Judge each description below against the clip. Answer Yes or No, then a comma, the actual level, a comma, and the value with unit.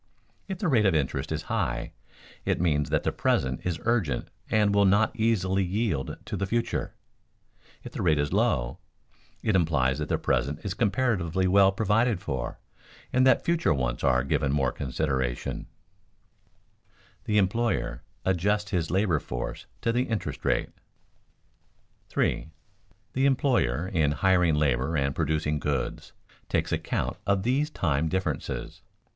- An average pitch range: No, wide, 6.8 semitones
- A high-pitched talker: No, very low, 90 Hz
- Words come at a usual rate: Yes, average, 145 wpm